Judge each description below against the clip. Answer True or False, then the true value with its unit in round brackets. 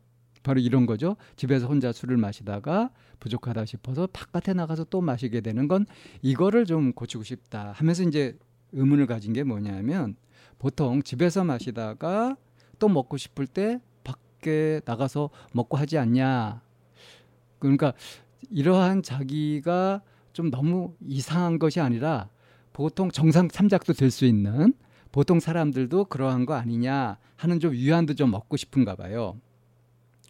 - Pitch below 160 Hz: True (135 Hz)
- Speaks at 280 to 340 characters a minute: True (285 characters per minute)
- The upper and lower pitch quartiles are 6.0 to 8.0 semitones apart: False (5.5 semitones)